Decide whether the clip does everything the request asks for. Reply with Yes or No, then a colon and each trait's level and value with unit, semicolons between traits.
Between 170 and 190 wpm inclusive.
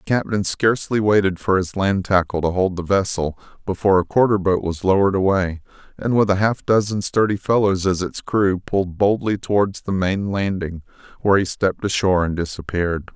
Yes: average, 185 wpm